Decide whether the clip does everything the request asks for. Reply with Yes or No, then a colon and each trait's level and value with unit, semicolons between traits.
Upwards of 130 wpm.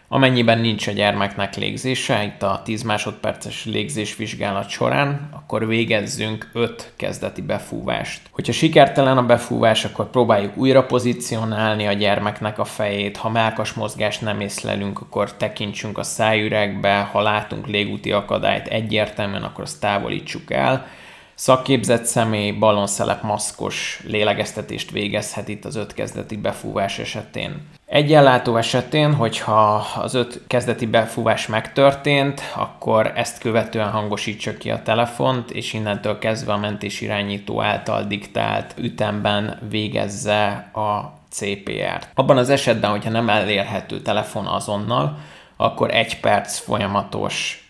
No: average, 125 wpm